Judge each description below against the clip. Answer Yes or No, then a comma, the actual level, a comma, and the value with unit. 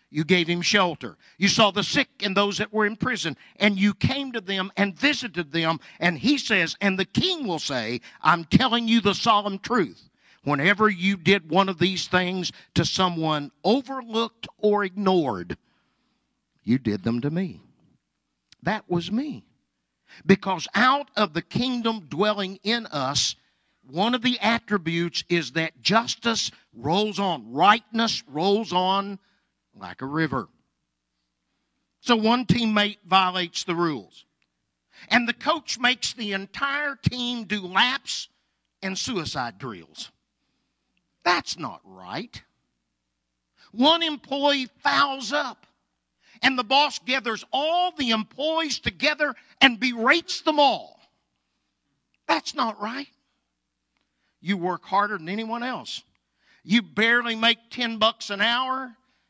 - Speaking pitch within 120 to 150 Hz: No, high, 205 Hz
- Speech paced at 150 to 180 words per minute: No, slow, 135 wpm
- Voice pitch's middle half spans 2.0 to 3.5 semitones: No, wide, 5.4 semitones